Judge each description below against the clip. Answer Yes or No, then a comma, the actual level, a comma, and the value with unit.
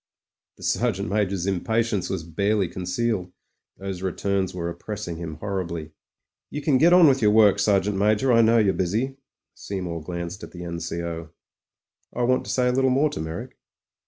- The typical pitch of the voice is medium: No, low, 100 Hz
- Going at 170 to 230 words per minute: Yes, average, 175 wpm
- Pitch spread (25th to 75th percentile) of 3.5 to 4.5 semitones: No, average, 4.9 semitones